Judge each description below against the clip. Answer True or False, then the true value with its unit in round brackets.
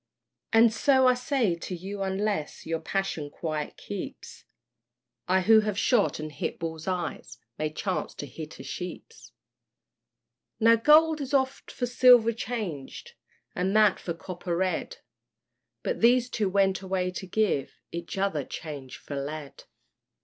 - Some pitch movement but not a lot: False (5.8 semitones)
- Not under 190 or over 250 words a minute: False (145 wpm)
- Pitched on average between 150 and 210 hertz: True (190 Hz)